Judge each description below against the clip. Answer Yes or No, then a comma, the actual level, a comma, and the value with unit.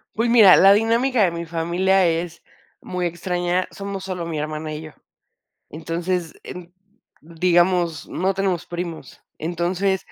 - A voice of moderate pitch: Yes, medium, 175 Hz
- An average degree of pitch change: No, narrow, 2.2 semitones